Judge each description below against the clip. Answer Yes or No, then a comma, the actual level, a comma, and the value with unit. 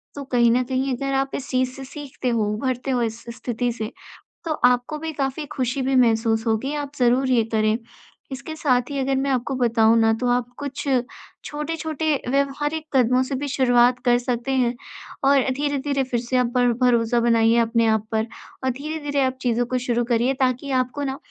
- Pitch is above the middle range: Yes, very high, 255 Hz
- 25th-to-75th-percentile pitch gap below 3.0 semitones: Yes, narrow, 2.4 semitones